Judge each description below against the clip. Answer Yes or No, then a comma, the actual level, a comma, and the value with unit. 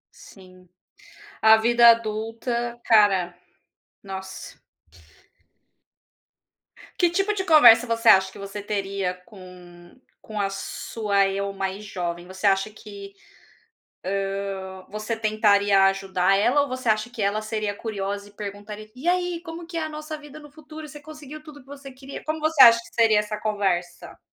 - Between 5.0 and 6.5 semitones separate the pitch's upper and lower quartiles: Yes, average, 5.3 semitones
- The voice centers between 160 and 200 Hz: No, high, 215 Hz